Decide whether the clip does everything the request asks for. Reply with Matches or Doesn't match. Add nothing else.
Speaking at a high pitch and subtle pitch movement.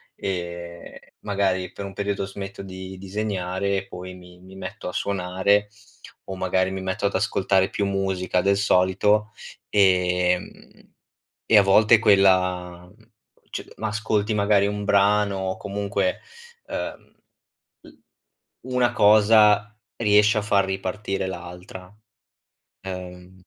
Doesn't match